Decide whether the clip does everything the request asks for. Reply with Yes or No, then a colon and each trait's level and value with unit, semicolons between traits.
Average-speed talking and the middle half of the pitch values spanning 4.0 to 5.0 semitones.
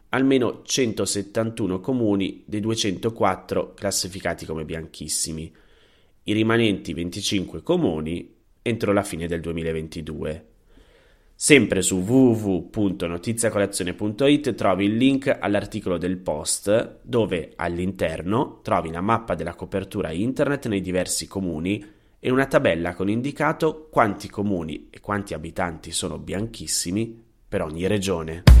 No: slow, 110 wpm; average, 4.3 semitones